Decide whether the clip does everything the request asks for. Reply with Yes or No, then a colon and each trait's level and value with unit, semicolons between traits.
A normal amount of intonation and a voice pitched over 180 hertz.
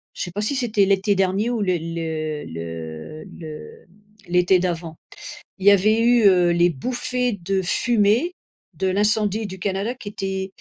Yes: average, 3.7 semitones; high, 190 Hz